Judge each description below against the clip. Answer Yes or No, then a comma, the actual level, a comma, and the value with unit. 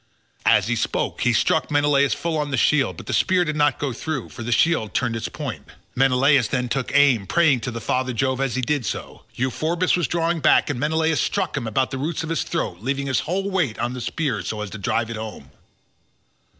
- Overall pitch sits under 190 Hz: Yes, low, 135 Hz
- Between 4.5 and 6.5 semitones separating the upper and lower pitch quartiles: Yes, average, 4.8 semitones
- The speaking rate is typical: No, fast, 225 wpm